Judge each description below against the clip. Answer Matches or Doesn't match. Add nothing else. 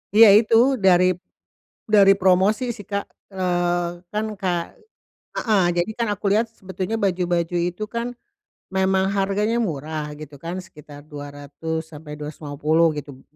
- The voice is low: Doesn't match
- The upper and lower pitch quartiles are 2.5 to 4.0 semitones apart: Doesn't match